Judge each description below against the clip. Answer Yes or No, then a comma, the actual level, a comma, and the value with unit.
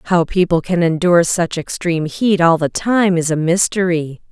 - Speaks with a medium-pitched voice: Yes, medium, 170 Hz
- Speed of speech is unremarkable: Yes, average, 180 wpm